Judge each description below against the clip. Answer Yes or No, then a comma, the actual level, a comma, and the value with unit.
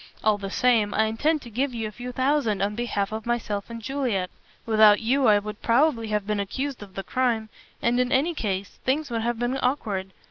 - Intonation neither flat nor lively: Yes, average, 3.4 semitones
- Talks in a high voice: Yes, high, 230 Hz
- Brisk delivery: Yes, fast, 215 wpm